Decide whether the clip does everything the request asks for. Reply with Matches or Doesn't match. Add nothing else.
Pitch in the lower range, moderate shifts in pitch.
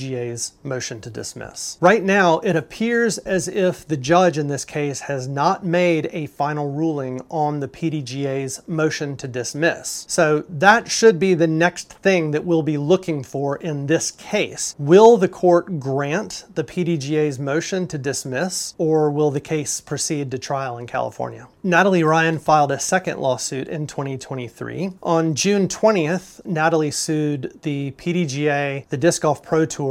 Doesn't match